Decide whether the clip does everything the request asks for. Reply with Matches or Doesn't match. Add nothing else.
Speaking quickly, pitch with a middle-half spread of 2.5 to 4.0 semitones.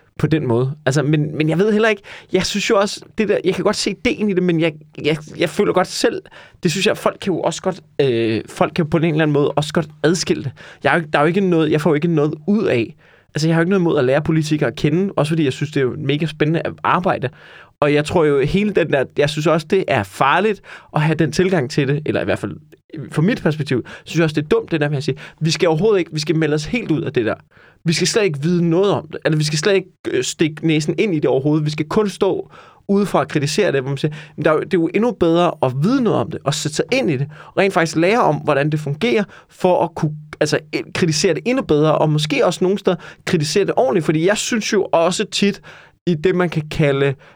Matches